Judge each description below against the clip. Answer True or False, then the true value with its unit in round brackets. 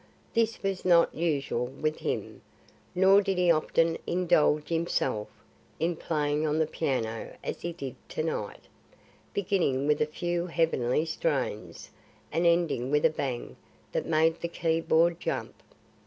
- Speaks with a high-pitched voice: False (160 Hz)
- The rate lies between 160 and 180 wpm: False (145 wpm)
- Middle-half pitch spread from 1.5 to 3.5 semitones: True (2.9 semitones)